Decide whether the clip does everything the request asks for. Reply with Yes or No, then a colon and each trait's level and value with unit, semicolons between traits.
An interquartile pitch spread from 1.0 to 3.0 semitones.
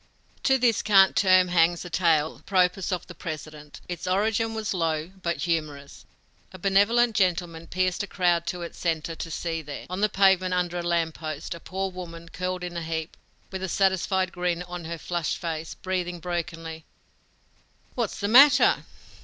Yes: narrow, 2.4 semitones